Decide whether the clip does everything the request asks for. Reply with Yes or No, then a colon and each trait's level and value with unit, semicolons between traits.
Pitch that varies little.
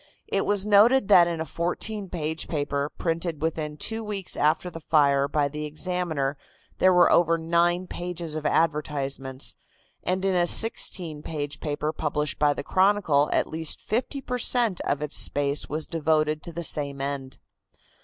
No: average, 3.4 semitones